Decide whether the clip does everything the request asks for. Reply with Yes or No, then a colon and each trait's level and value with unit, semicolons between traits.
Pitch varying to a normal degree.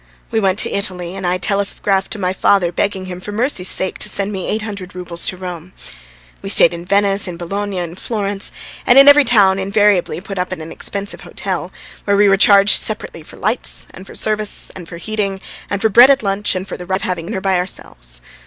No: narrow, 2.1 semitones